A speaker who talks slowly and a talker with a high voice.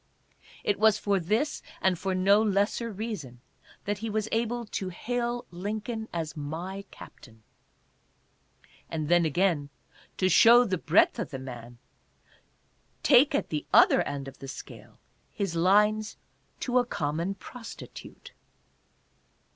Yes: slow, 130 wpm; high, 195 Hz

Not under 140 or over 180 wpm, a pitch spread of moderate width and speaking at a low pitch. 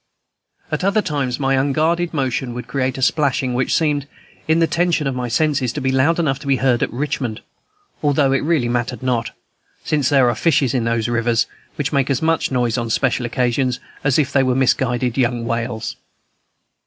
No: average, 190 wpm; average, 3.1 semitones; low, 130 Hz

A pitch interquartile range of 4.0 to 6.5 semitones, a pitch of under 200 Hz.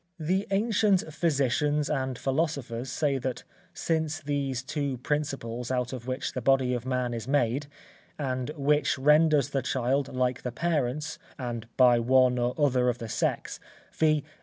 No: average, 3.1 semitones; low, 135 Hz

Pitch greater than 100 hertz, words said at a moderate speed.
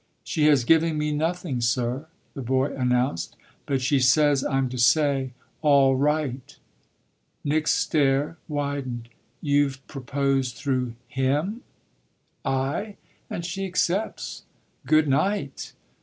No: medium, 140 Hz; slow, 110 wpm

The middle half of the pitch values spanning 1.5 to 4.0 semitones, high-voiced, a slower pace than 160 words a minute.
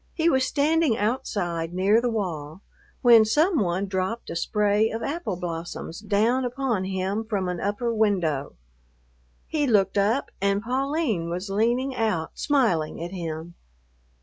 No: average, 5.2 semitones; high, 210 Hz; average, 145 wpm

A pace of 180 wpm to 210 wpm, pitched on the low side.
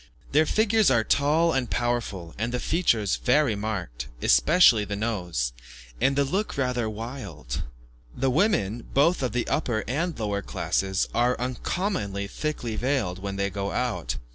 No: average, 145 wpm; low, 120 Hz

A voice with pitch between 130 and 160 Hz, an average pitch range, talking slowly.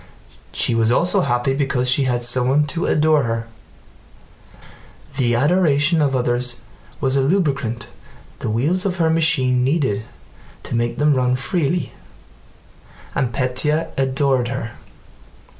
Yes: low, 135 Hz; average, 3.6 semitones; slow, 125 wpm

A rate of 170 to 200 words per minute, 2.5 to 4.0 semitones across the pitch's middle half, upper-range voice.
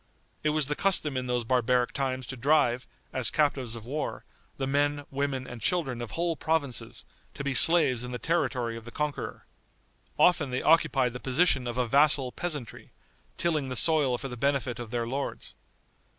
No: average, 180 wpm; average, 3.3 semitones; low, 135 Hz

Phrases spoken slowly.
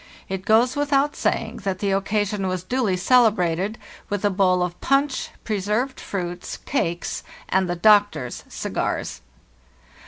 Yes: slow, 130 wpm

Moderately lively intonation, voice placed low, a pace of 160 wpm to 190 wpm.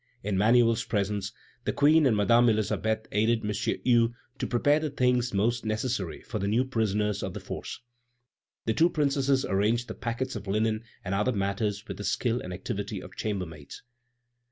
Yes: average, 3.2 semitones; low, 110 Hz; average, 175 wpm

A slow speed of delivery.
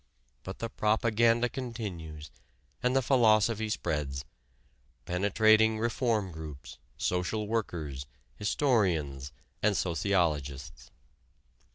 Yes: slow, 80 wpm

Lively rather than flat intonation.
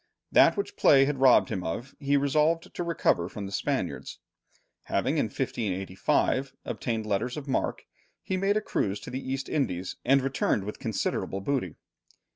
Yes: wide, 6.1 semitones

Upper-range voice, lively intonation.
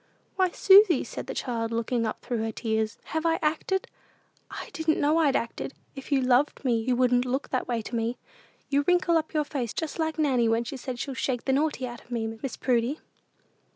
No: very high, 260 Hz; average, 4.6 semitones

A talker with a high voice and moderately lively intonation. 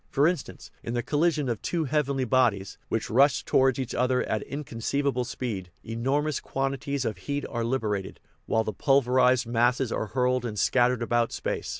No: low, 125 Hz; average, 3.1 semitones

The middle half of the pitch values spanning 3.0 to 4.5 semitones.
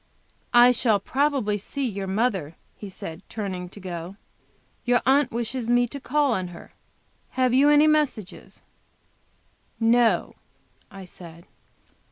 No: average, 5.2 semitones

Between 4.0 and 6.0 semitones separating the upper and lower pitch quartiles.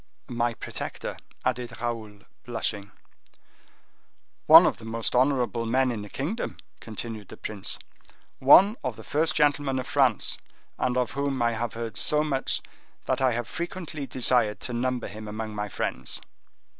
No: average, 3.4 semitones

